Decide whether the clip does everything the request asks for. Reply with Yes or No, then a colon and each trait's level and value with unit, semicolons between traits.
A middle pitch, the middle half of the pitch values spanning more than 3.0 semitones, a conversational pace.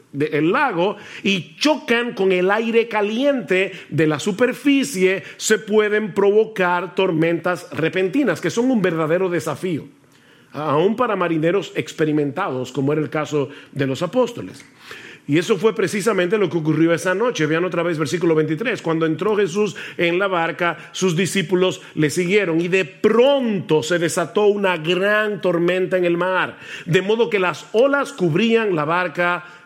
Yes: medium, 180 Hz; average, 4.0 semitones; average, 150 wpm